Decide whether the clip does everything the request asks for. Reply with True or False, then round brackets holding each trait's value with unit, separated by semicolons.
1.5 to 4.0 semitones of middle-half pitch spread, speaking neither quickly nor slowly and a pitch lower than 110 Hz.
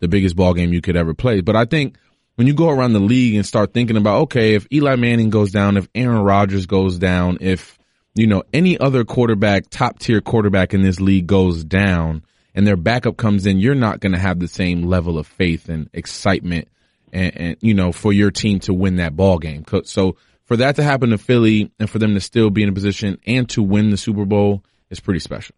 False (3.5 semitones; 235 wpm; 100 Hz)